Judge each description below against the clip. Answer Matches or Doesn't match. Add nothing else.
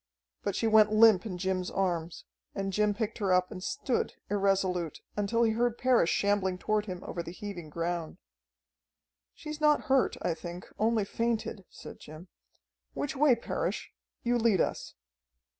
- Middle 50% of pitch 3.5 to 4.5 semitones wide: Matches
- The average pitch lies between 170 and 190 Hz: Doesn't match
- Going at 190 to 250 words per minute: Doesn't match